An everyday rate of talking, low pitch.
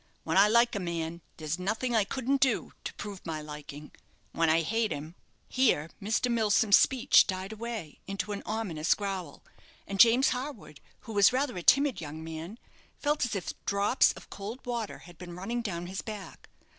No: average, 185 wpm; high, 200 Hz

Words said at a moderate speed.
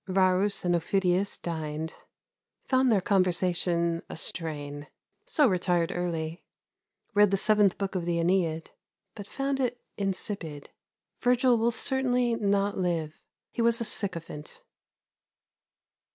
No: slow, 120 wpm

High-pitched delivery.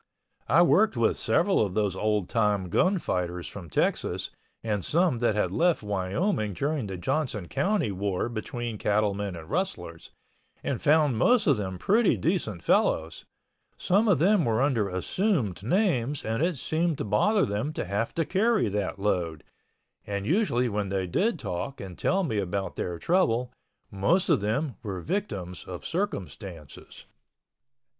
No: low, 110 Hz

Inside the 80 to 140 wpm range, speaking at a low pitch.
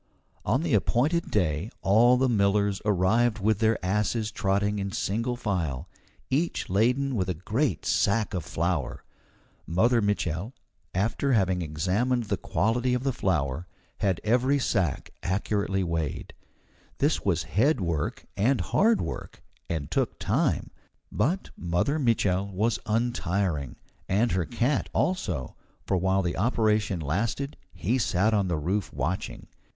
Yes: slow, 135 wpm; low, 105 Hz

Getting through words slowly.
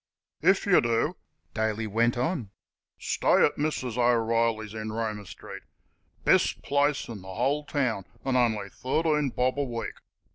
No: average, 145 wpm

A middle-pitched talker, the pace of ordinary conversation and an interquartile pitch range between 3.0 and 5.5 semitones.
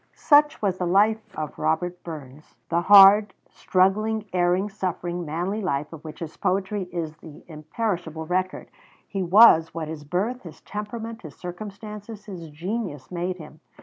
Yes: medium, 180 Hz; average, 155 wpm; average, 4.2 semitones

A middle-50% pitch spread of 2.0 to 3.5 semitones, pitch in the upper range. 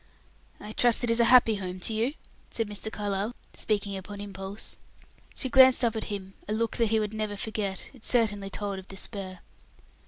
Yes: narrow, 2.4 semitones; high, 210 Hz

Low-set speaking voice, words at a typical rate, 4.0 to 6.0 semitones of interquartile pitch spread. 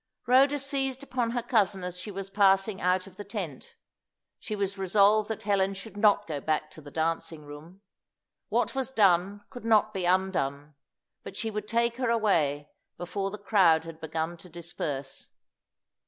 No: high, 195 Hz; average, 170 wpm; average, 4.4 semitones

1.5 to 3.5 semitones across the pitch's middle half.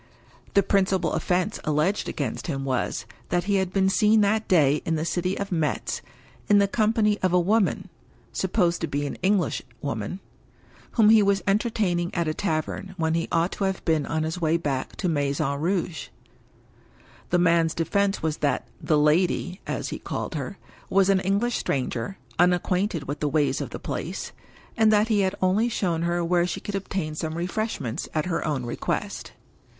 No: average, 4.1 semitones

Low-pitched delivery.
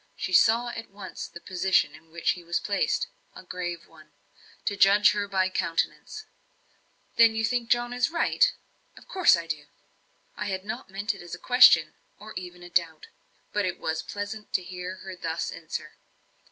No: high, 190 Hz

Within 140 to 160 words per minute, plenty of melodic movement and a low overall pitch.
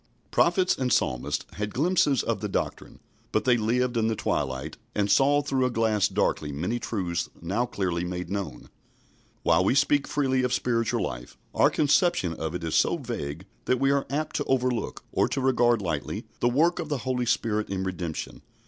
No: average, 185 wpm; wide, 6.8 semitones; low, 115 Hz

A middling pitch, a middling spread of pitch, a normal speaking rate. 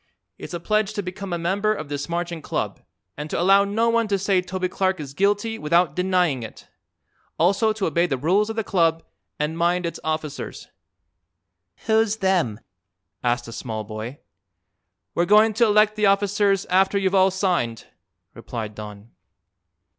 Yes: medium, 180 Hz; average, 4.7 semitones; average, 165 wpm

